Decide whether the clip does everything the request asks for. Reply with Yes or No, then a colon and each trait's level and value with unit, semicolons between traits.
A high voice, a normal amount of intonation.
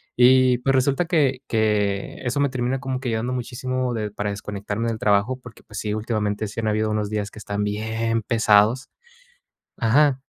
No: low, 115 Hz; average, 3.3 semitones